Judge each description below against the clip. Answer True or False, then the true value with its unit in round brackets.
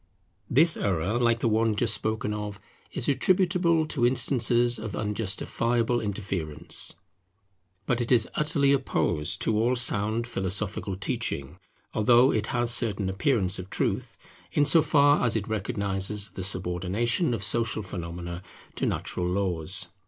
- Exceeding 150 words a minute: False (140 wpm)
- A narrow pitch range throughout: False (4.0 semitones)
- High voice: False (110 Hz)